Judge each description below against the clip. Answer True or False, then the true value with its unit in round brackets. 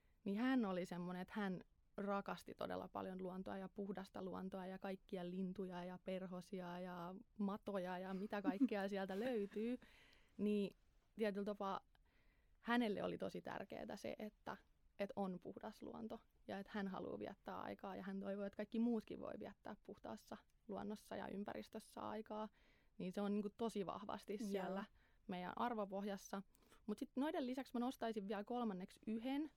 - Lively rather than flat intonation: False (2.5 semitones)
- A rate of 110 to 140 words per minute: False (150 wpm)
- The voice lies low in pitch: False (200 Hz)